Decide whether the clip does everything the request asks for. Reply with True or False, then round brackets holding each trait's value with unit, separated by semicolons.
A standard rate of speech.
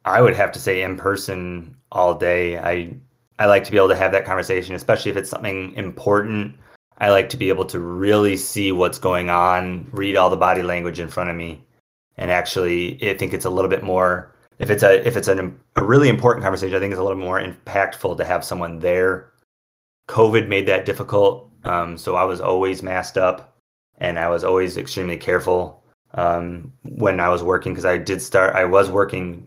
False (210 wpm)